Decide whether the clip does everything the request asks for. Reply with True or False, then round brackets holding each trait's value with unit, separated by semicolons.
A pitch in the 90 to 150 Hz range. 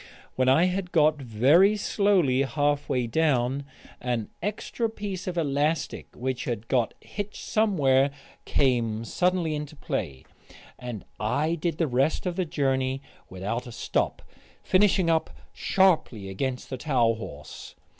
True (140 Hz)